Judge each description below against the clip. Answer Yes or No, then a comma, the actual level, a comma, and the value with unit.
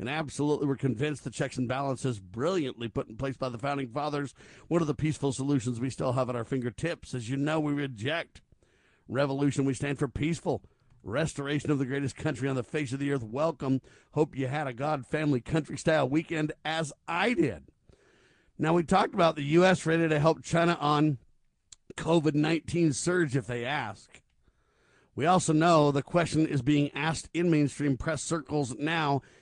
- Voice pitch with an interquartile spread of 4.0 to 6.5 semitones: No, average, 2.8 semitones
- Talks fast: No, average, 185 wpm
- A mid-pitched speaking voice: Yes, medium, 145 Hz